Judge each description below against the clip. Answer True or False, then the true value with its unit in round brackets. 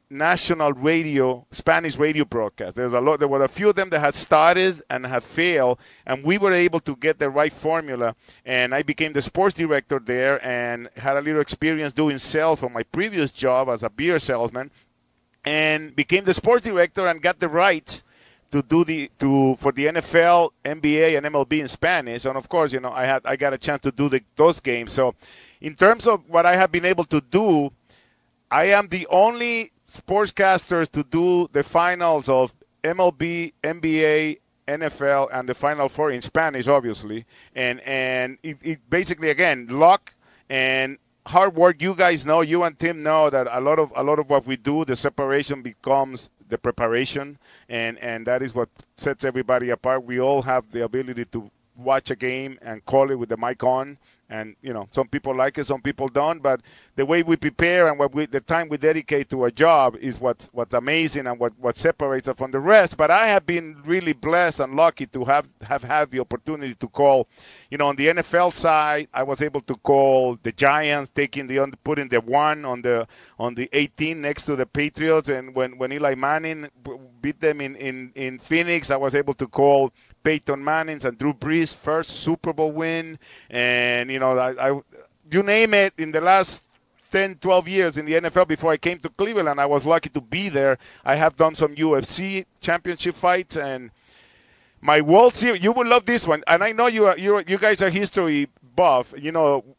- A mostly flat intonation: False (3.9 semitones)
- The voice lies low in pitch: False (145 Hz)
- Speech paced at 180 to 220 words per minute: True (205 wpm)